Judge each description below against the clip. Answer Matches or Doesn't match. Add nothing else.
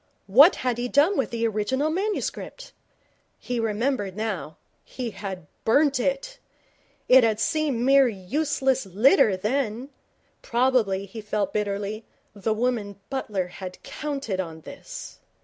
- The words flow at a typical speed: Doesn't match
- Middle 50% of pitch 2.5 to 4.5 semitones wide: Doesn't match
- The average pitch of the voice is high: Matches